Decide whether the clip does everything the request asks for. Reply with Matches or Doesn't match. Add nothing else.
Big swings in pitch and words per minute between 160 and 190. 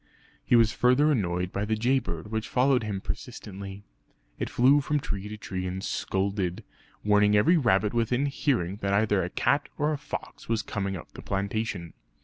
Doesn't match